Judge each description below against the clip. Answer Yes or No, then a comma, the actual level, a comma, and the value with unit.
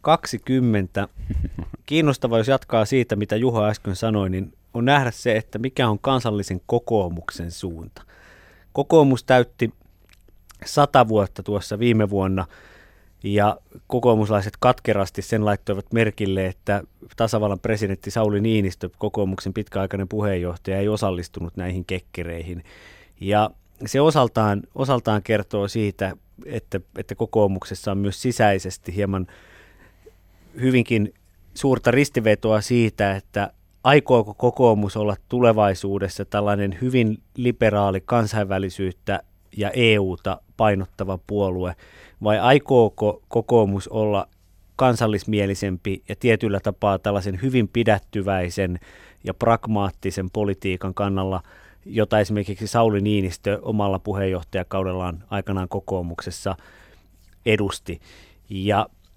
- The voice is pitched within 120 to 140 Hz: No, low, 100 Hz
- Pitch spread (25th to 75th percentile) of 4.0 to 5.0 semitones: No, average, 3.1 semitones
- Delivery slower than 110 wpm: Yes, average, 100 wpm